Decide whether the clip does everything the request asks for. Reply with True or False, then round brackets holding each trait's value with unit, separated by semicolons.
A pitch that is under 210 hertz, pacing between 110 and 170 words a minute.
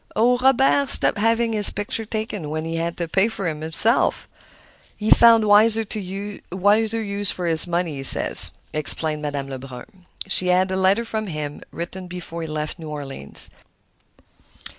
True (185 Hz; 160 wpm)